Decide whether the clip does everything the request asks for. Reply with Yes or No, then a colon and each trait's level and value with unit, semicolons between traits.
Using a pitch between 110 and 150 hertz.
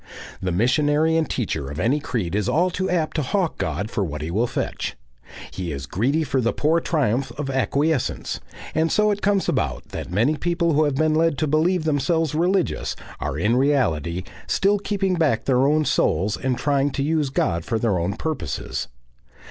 Yes: medium, 140 Hz